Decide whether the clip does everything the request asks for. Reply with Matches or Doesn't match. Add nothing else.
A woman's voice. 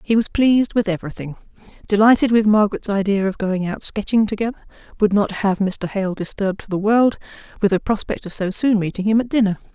Matches